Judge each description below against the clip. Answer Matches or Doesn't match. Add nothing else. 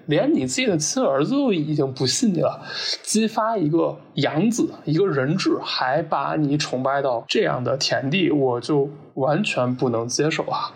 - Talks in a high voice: Doesn't match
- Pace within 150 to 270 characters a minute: Matches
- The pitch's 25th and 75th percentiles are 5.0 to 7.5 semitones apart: Doesn't match